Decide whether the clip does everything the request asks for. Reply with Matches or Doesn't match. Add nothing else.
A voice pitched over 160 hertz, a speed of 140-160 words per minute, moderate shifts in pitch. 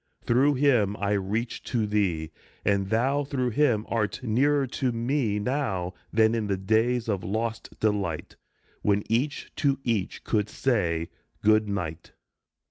Doesn't match